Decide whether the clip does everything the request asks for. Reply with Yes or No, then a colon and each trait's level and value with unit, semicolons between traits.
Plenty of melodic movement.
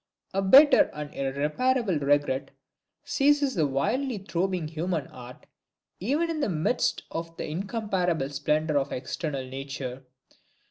Yes: wide, 6.7 semitones